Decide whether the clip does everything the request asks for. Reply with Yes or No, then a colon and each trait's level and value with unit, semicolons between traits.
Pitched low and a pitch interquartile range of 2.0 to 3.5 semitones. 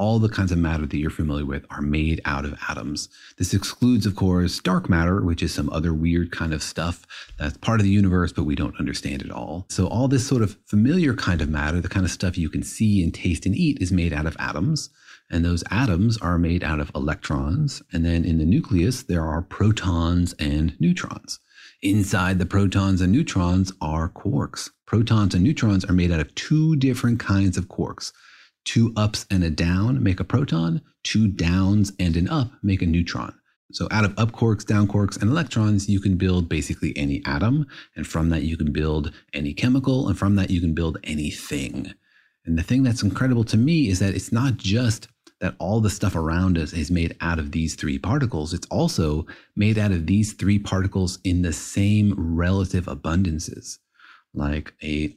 No: very low, 95 Hz; average, 4.2 semitones